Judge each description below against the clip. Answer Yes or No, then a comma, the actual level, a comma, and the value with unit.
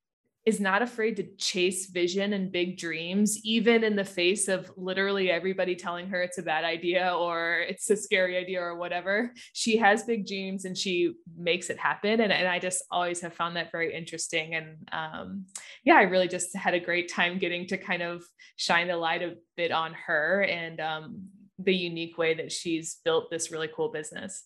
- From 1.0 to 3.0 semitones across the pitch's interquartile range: Yes, narrow, 2.4 semitones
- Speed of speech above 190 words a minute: Yes, average, 200 wpm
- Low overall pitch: No, medium, 180 Hz